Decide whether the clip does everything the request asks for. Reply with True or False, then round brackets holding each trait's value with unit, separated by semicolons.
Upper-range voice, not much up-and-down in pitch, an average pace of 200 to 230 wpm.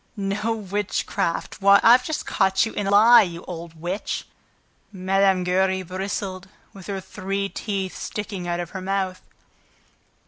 False (195 Hz; 1.6 semitones; 145 wpm)